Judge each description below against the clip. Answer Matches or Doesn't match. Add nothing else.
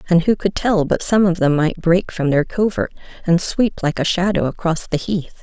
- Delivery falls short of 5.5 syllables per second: Matches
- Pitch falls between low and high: Matches